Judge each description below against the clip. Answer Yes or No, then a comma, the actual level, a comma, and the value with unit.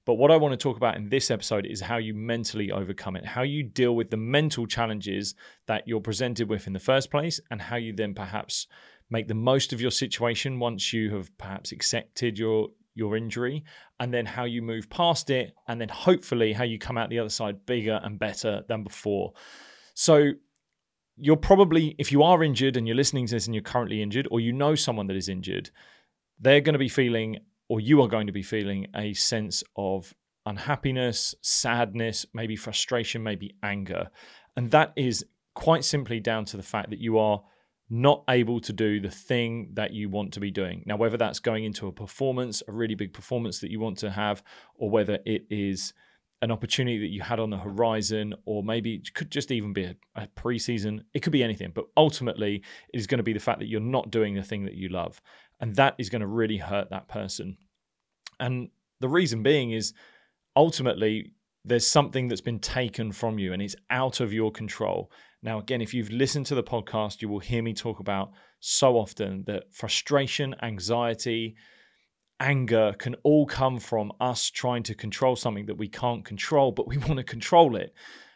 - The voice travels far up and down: No, average, 3.3 semitones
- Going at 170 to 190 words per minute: No, fast, 205 wpm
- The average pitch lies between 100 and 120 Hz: Yes, low, 115 Hz